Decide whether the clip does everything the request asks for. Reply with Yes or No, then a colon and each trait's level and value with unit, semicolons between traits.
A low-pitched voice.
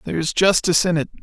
No: medium, 170 Hz